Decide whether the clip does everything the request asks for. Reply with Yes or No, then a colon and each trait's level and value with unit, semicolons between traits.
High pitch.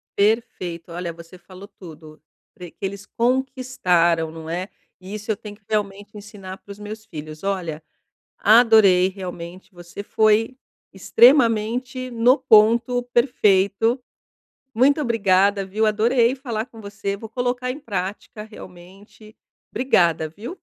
Yes: high, 205 Hz